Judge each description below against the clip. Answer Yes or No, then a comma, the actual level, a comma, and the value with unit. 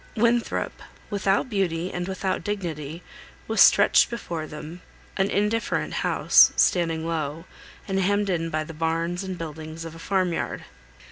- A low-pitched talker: No, medium, 175 Hz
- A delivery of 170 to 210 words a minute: No, average, 145 wpm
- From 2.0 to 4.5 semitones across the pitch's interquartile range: Yes, average, 3.1 semitones